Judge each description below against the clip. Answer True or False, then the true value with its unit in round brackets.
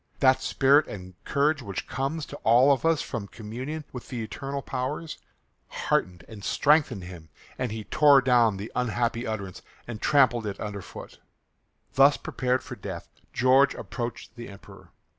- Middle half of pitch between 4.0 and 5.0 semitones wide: True (4.3 semitones)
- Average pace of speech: True (160 wpm)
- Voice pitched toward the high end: False (125 Hz)